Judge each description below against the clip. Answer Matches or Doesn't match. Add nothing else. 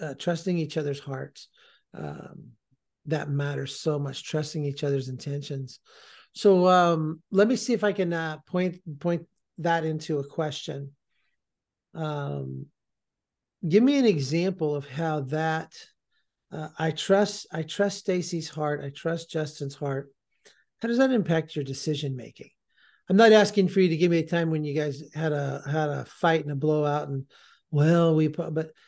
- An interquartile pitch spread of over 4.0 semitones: Doesn't match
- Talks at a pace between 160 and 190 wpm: Matches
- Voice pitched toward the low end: Doesn't match